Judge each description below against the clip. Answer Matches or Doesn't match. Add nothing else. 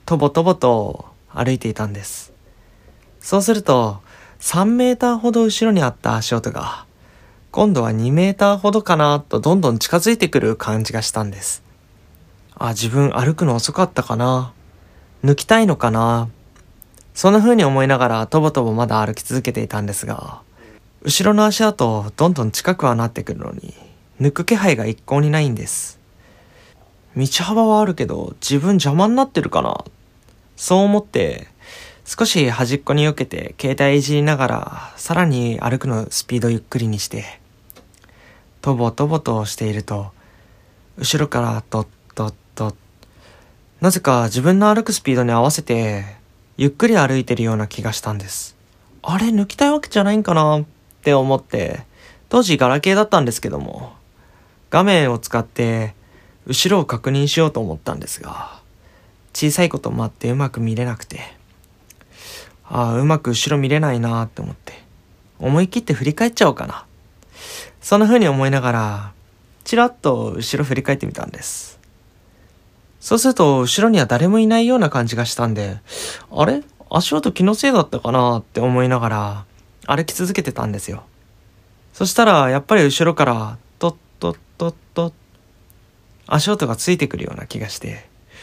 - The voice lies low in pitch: Matches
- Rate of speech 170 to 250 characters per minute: Doesn't match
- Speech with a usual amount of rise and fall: Doesn't match